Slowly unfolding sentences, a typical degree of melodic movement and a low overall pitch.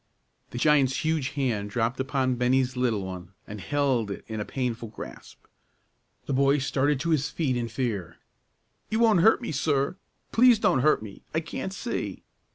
No: average, 170 wpm; average, 4.3 semitones; low, 130 Hz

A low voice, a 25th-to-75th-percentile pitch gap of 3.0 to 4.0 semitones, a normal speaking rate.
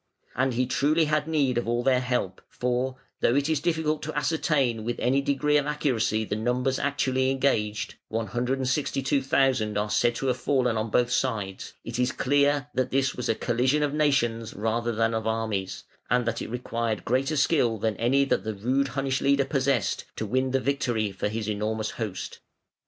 Yes: low, 125 Hz; average, 3.5 semitones; average, 185 wpm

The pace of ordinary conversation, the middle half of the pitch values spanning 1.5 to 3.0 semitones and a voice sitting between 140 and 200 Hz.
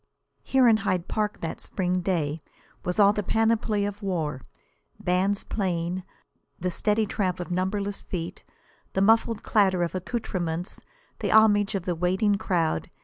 Yes: average, 145 wpm; average, 2.7 semitones; high, 190 Hz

